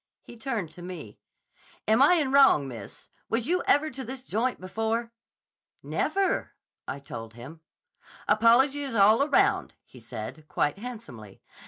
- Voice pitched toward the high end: Yes, high, 225 Hz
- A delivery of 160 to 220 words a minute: No, average, 140 wpm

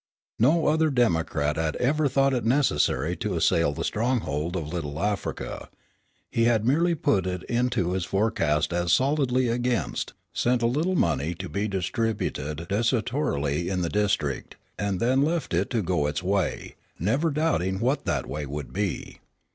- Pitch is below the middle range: Yes, low, 100 Hz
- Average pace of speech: Yes, average, 160 wpm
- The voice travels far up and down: Yes, wide, 7.1 semitones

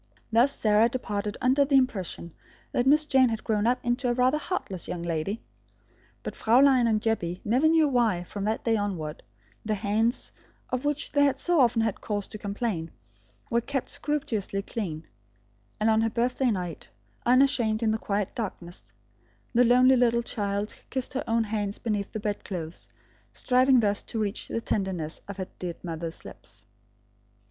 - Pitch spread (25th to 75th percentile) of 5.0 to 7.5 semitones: No, average, 3.9 semitones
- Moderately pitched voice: No, high, 225 Hz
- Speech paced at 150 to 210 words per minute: Yes, average, 170 wpm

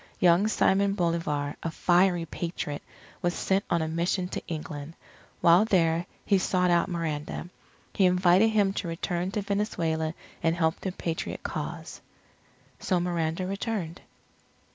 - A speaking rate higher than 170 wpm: No, average, 140 wpm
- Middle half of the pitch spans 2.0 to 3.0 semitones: Yes, narrow, 2.6 semitones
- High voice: No, medium, 175 Hz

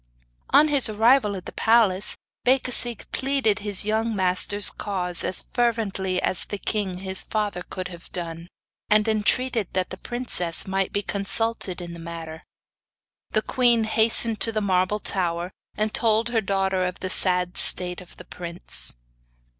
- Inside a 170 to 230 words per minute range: No, average, 155 wpm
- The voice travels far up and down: No, average, 3.7 semitones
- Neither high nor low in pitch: No, high, 200 Hz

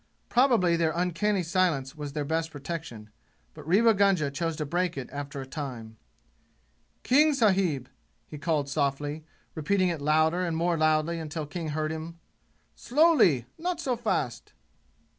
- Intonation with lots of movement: No, average, 4.2 semitones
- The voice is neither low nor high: Yes, medium, 160 Hz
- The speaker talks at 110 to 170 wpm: Yes, average, 145 wpm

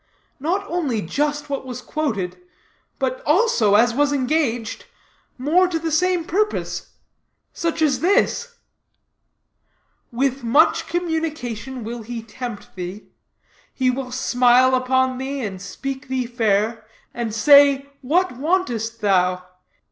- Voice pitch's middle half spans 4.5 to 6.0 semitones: Yes, average, 5.0 semitones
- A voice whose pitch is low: No, very high, 260 Hz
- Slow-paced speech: Yes, slow, 120 wpm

